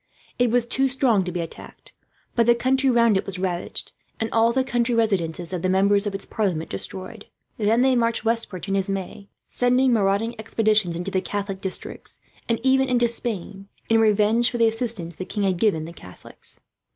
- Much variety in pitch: No, average, 3.7 semitones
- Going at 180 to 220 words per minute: Yes, average, 190 wpm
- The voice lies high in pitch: Yes, high, 215 Hz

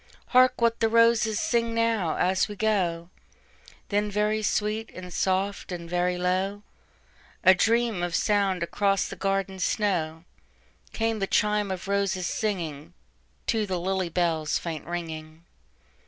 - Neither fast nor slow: No, slow, 125 wpm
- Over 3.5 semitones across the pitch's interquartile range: No, average, 3.2 semitones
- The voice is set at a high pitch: Yes, high, 195 Hz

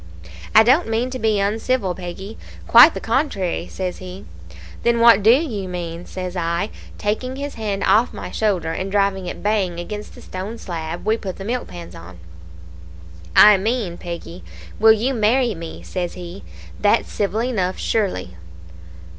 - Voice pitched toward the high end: Yes, high, 200 Hz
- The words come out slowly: No, average, 165 wpm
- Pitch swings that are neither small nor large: Yes, average, 4.0 semitones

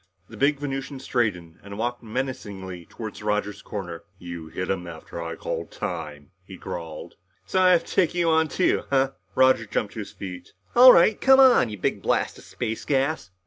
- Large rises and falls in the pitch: Yes, wide, 7.5 semitones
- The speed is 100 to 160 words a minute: No, average, 190 wpm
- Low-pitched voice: Yes, low, 110 Hz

